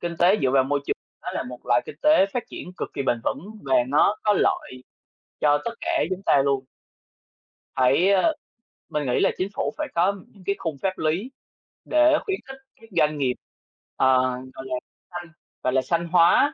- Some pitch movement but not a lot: No, wide, 6.8 semitones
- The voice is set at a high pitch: No, medium, 170 Hz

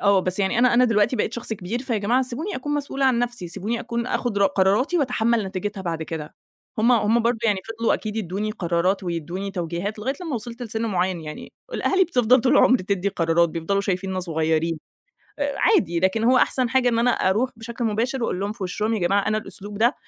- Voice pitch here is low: No, high, 215 Hz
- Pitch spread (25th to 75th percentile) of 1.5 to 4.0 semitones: No, average, 4.5 semitones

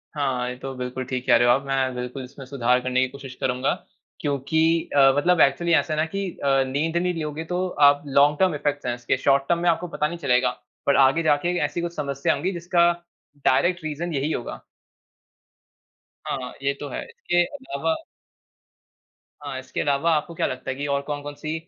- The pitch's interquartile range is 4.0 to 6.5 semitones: No, average, 3.6 semitones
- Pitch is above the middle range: No, medium, 145 Hz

